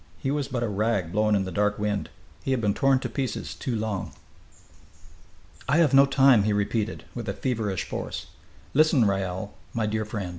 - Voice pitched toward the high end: No, low, 110 Hz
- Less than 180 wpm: No, average, 190 wpm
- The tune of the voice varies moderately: Yes, average, 4.4 semitones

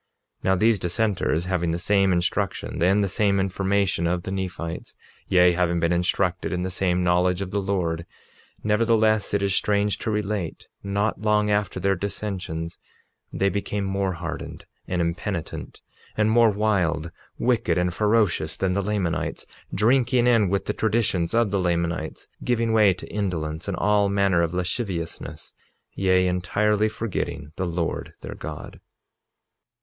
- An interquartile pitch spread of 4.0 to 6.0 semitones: No, average, 3.1 semitones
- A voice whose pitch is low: Yes, very low, 95 Hz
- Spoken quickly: No, average, 150 wpm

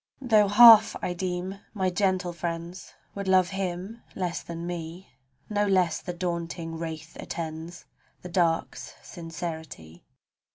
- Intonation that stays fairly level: Yes, narrow, 2.3 semitones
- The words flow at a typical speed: No, slow, 125 wpm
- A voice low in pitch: No, medium, 175 Hz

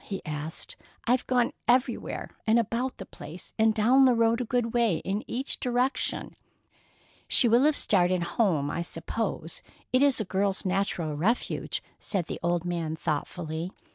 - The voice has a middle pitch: No, high, 205 Hz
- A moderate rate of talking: Yes, average, 150 wpm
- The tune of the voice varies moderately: No, wide, 5.9 semitones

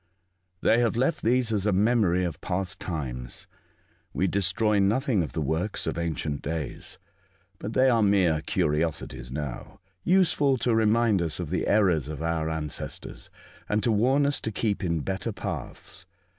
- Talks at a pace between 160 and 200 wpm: Yes, average, 165 wpm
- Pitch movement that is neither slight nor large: No, wide, 5.8 semitones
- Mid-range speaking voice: No, very low, 95 Hz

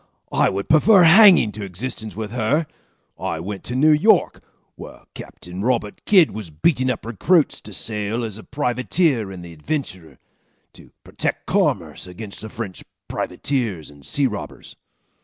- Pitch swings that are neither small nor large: No, wide, 6.4 semitones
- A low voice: Yes, low, 110 Hz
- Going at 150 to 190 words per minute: Yes, average, 155 wpm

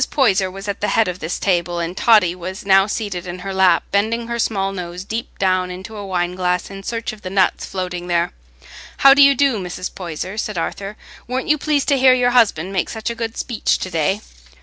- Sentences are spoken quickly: Yes, fast, 225 wpm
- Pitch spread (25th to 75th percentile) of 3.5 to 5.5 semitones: Yes, average, 3.8 semitones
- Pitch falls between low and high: No, high, 195 Hz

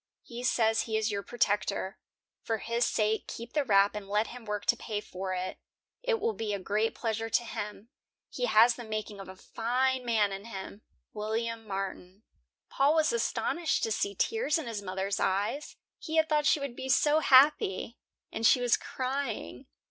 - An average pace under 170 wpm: No, average, 185 wpm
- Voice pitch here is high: Yes, high, 225 Hz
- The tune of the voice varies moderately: Yes, average, 4.0 semitones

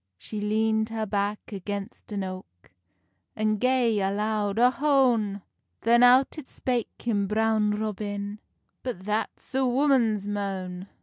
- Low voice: No, high, 215 Hz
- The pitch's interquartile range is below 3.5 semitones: Yes, average, 2.8 semitones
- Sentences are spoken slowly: Yes, slow, 130 wpm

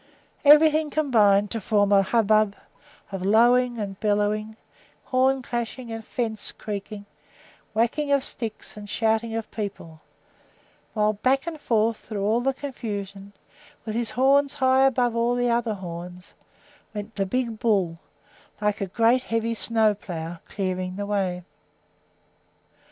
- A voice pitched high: Yes, high, 220 Hz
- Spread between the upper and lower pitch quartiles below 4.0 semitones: Yes, average, 3.2 semitones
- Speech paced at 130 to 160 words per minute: Yes, slow, 135 wpm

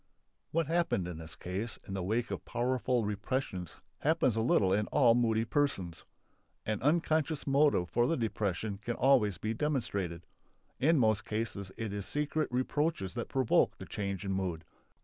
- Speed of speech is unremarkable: Yes, average, 165 wpm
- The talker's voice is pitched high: No, low, 115 Hz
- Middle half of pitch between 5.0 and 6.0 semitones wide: Yes, wide, 5.6 semitones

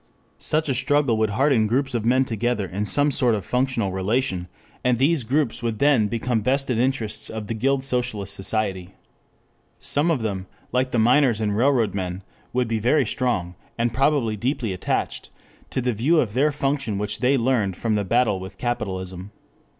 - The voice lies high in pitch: No, low, 120 Hz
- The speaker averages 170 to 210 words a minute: Yes, average, 180 wpm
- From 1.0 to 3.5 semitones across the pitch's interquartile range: No, average, 4.2 semitones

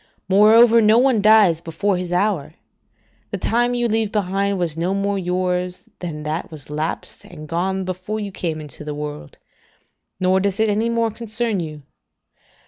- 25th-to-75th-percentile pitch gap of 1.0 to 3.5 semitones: No, average, 4.3 semitones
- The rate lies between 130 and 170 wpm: Yes, average, 165 wpm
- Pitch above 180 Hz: Yes, high, 190 Hz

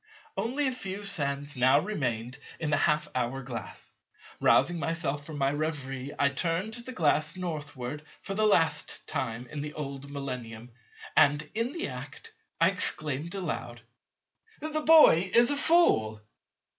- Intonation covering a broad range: Yes, wide, 6.1 semitones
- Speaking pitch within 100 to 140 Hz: No, medium, 150 Hz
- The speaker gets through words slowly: No, average, 145 wpm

